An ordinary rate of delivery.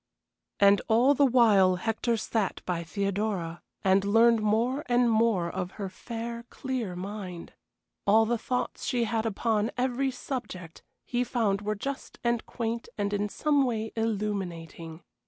Yes: average, 145 wpm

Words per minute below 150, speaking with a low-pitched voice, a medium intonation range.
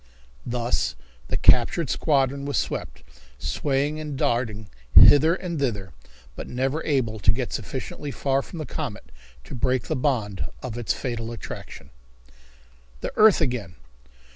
Yes: average, 140 wpm; low, 130 Hz; average, 3.9 semitones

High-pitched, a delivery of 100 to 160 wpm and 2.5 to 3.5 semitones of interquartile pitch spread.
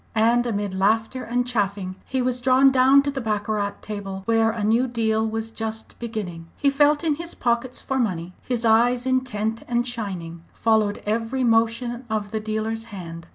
No: high, 225 Hz; average, 175 wpm; average, 2.9 semitones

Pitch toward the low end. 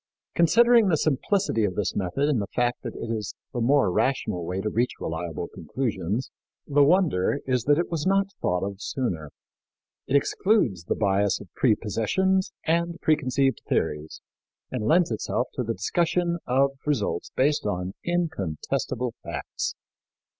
Yes: low, 125 Hz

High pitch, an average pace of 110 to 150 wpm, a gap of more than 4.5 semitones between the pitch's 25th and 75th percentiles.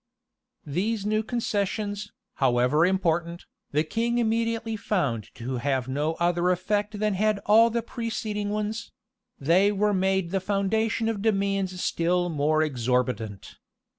Yes: high, 195 Hz; slow, 135 wpm; average, 5.3 semitones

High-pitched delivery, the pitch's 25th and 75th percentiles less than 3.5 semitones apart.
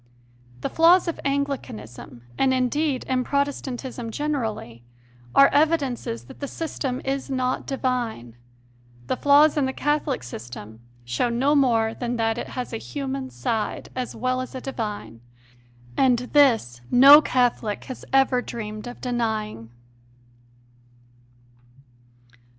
No: very high, 255 Hz; average, 3.8 semitones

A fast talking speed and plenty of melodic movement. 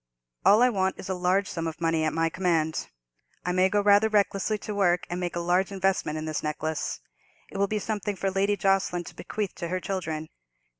No: fast, 215 wpm; average, 3.1 semitones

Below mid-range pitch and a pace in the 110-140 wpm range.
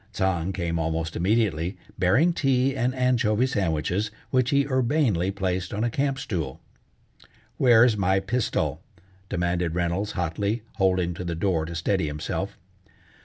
Yes: very low, 95 Hz; slow, 135 wpm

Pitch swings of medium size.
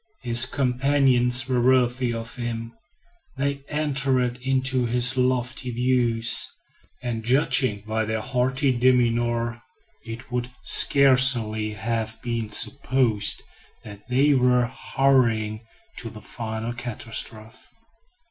No: narrow, 2.1 semitones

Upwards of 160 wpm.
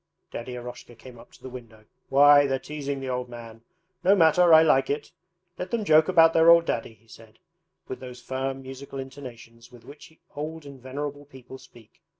Yes: average, 190 wpm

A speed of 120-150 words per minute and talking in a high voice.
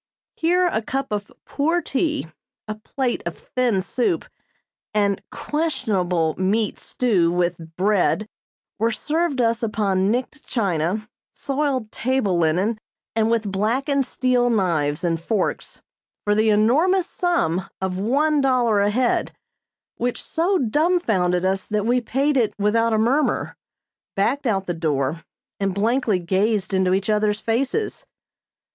Yes: slow, 135 wpm; high, 220 Hz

